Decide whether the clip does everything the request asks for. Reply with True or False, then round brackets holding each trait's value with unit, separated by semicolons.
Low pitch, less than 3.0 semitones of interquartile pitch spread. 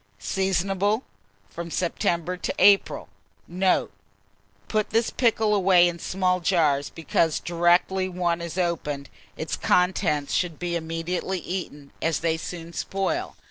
False (175 Hz; 2.5 semitones)